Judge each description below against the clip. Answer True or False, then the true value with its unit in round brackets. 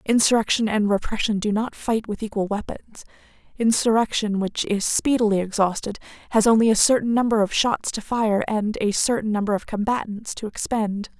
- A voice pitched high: True (215 Hz)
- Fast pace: False (165 wpm)